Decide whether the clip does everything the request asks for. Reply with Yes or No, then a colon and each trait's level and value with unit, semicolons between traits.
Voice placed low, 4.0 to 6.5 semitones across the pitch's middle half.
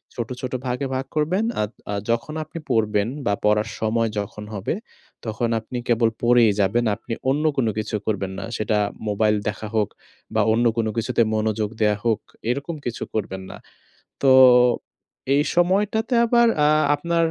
Yes: low, 115 Hz; average, 4.7 semitones